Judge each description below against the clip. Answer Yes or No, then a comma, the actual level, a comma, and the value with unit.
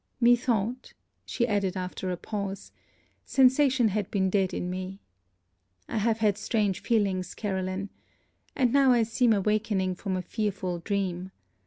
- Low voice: No, high, 205 Hz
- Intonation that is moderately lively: Yes, average, 3.4 semitones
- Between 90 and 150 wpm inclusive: Yes, average, 145 wpm